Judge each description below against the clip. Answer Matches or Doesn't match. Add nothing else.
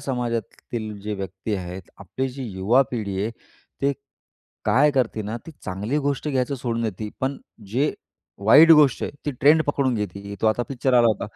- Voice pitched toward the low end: Matches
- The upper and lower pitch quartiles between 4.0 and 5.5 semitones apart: Matches